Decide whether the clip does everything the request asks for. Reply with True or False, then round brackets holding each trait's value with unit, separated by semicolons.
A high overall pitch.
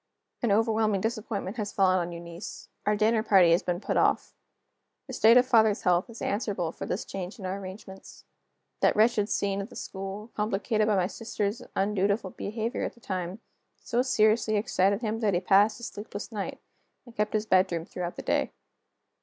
True (205 Hz)